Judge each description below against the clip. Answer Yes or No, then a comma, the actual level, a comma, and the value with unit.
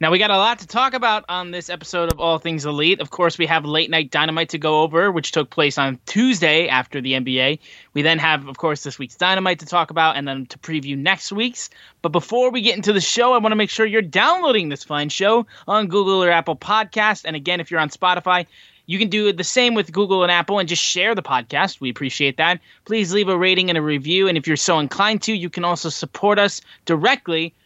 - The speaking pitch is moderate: Yes, medium, 175 Hz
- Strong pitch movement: No, average, 4.4 semitones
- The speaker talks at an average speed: No, fast, 245 wpm